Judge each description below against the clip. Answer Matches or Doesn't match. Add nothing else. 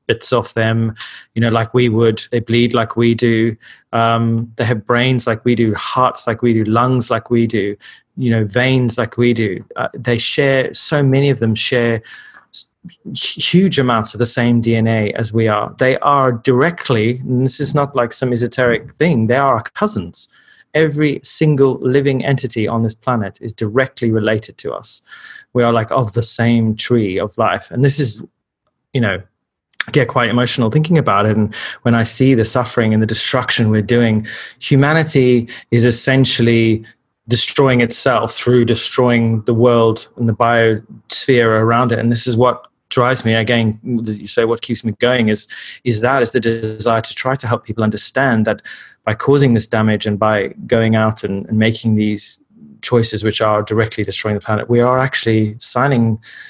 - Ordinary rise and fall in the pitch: Doesn't match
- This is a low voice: Matches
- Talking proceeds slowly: Doesn't match